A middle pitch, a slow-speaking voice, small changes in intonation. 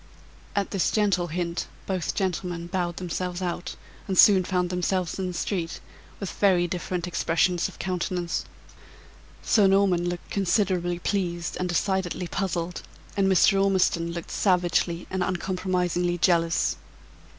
Yes: medium, 180 Hz; slow, 130 wpm; narrow, 1.5 semitones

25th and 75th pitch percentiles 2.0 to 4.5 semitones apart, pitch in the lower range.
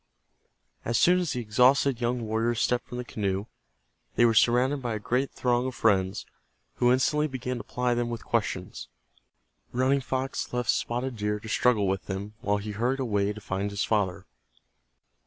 Yes: average, 3.2 semitones; low, 120 Hz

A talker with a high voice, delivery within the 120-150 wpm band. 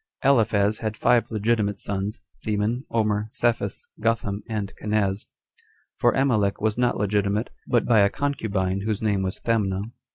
No: low, 105 Hz; average, 140 wpm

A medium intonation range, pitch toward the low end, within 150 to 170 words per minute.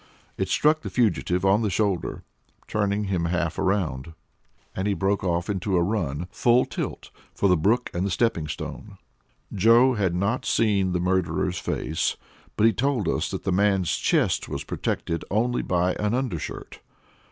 Yes: average, 3.7 semitones; low, 100 Hz; average, 165 wpm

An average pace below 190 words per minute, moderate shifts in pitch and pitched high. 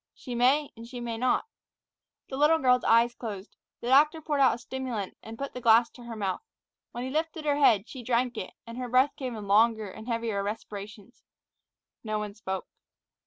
No: average, 200 wpm; average, 3.1 semitones; high, 240 Hz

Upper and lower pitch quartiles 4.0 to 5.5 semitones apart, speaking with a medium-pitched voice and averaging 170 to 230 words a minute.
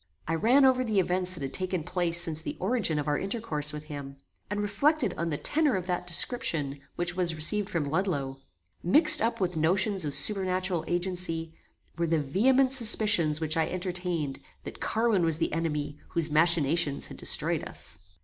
Yes: average, 4.3 semitones; medium, 175 Hz; average, 180 wpm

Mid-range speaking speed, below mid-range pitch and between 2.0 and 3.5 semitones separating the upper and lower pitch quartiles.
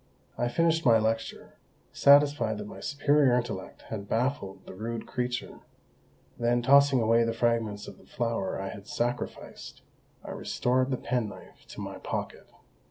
Yes: average, 145 wpm; low, 120 Hz; average, 2.8 semitones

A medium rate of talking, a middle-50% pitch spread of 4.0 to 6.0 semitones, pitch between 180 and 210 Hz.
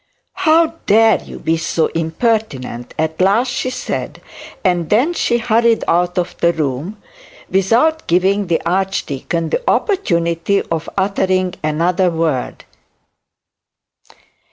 No: slow, 110 wpm; average, 5.1 semitones; medium, 185 Hz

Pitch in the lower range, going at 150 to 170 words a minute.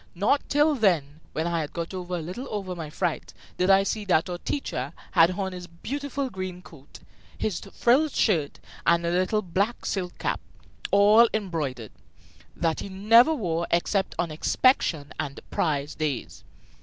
No: medium, 180 Hz; average, 160 wpm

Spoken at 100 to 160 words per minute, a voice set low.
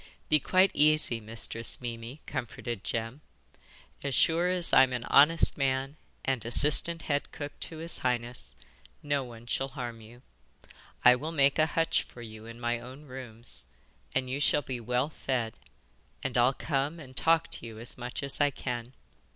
No: average, 170 wpm; low, 130 Hz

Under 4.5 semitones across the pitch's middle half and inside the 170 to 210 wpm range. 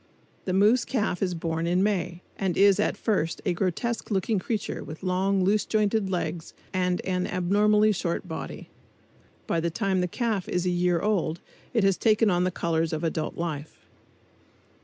Yes: average, 3.2 semitones; average, 175 wpm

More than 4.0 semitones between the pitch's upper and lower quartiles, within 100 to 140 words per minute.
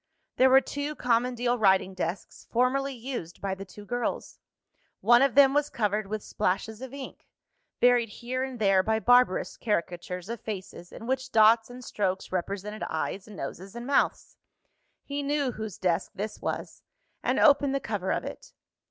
No: average, 4.7 semitones; average, 170 wpm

